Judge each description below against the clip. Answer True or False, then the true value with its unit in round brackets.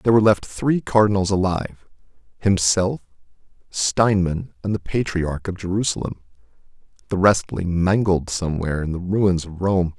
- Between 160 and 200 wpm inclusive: False (140 wpm)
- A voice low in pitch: True (95 Hz)